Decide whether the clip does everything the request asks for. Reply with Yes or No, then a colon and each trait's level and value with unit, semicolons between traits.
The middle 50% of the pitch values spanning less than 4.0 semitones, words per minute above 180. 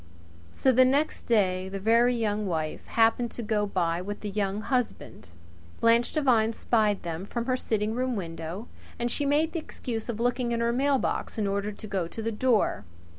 Yes: average, 3.4 semitones; average, 190 wpm